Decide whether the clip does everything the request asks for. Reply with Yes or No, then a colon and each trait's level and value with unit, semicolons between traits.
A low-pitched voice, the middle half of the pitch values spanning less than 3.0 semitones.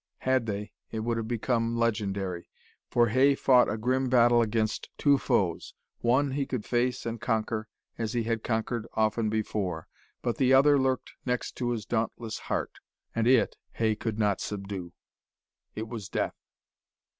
Yes: low, 115 Hz; narrow, 2.4 semitones